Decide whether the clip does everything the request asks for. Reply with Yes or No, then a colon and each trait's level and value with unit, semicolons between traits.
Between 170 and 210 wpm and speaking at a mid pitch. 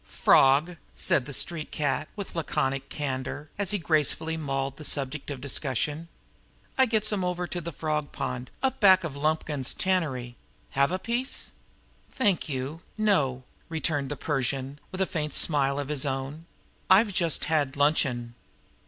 No: average, 155 wpm; medium, 150 Hz